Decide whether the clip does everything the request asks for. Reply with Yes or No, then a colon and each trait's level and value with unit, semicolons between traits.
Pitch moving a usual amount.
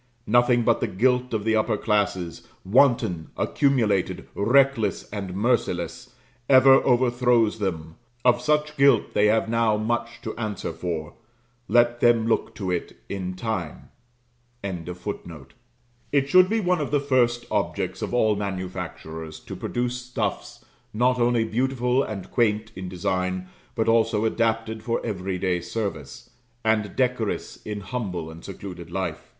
Yes: average, 4.4 semitones